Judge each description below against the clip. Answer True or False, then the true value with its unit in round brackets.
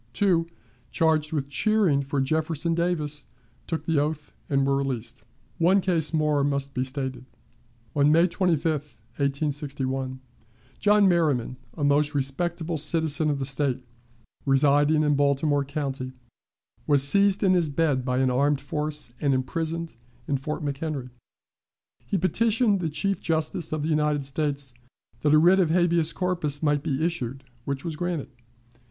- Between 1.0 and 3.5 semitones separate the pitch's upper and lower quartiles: True (3.0 semitones)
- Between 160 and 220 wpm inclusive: False (145 wpm)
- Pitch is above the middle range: False (150 Hz)